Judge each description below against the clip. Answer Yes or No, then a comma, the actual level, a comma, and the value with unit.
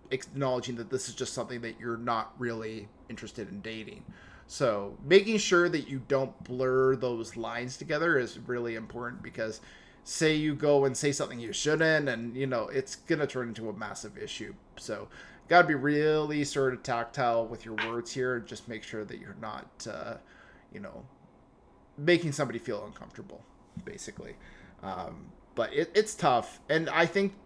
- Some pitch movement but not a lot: Yes, average, 4.1 semitones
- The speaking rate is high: No, average, 175 wpm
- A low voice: Yes, low, 130 Hz